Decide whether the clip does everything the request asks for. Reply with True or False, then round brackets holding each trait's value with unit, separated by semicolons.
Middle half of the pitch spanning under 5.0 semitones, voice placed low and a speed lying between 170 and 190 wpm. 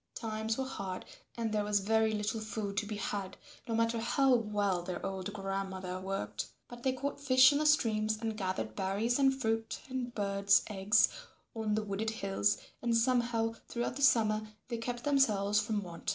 False (3.1 semitones; 215 Hz; 180 wpm)